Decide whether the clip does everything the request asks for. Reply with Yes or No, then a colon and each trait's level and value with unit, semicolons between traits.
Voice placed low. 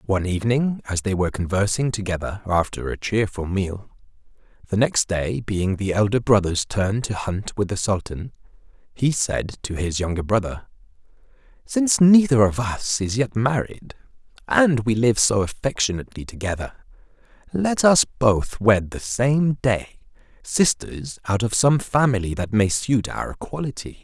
Yes: low, 110 Hz